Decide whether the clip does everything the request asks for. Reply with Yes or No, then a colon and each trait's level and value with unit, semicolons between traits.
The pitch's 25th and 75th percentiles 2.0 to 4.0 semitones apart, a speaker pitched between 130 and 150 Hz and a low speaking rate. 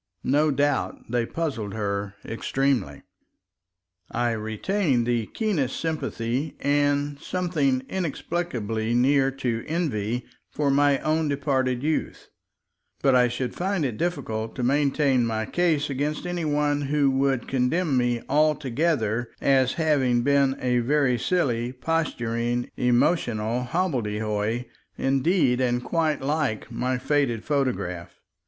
Yes: average, 3.7 semitones; low, 135 Hz; slow, 120 wpm